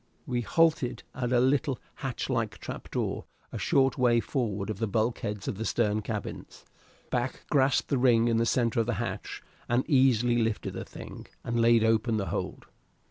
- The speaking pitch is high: No, low, 120 Hz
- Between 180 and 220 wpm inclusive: Yes, average, 185 wpm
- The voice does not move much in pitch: Yes, narrow, 2.3 semitones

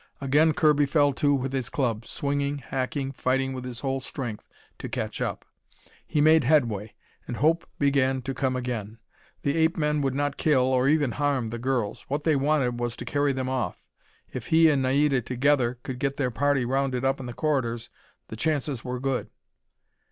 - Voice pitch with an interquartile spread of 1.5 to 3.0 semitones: Yes, narrow, 2.4 semitones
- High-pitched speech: No, low, 135 Hz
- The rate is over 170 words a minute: Yes, average, 190 wpm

